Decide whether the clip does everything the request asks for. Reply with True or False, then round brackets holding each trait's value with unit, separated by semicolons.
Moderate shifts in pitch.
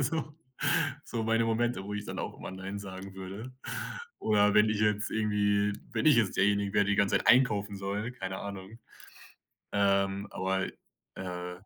False (2.1 semitones)